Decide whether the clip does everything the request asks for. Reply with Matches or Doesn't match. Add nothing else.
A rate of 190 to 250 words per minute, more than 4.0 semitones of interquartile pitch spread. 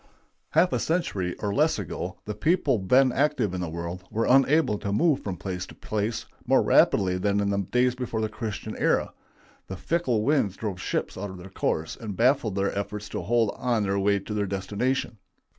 Matches